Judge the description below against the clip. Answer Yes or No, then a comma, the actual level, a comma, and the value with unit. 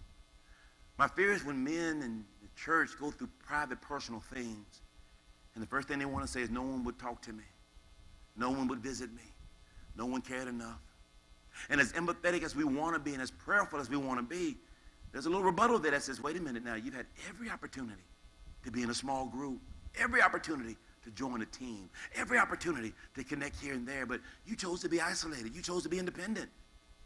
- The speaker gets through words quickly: Yes, fast, 215 wpm